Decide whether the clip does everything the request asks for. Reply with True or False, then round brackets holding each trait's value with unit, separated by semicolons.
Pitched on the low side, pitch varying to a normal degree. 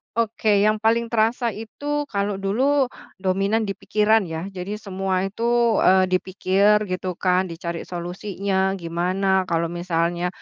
False (195 Hz; 3.0 semitones)